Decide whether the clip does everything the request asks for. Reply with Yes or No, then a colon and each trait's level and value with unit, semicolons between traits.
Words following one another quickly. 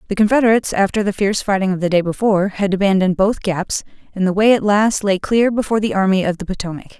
Yes: fast, 230 wpm